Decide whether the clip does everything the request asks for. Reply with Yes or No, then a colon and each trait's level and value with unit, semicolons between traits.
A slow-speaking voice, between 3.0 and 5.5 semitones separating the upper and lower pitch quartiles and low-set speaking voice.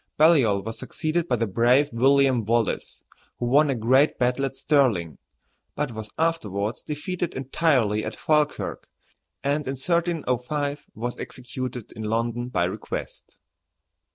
Yes: slow, 130 wpm; average, 4.3 semitones; low, 130 Hz